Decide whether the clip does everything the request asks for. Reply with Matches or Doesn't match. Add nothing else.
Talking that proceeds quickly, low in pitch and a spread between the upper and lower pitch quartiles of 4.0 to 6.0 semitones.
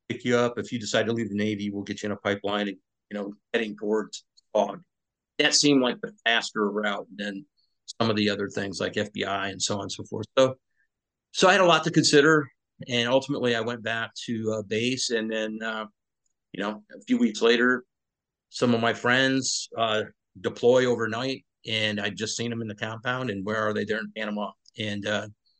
Doesn't match